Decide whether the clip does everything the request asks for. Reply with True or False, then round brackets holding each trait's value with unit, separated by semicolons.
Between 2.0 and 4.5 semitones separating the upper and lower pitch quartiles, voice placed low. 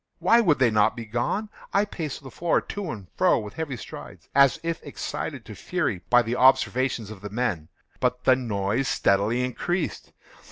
False (5.4 semitones; 125 Hz)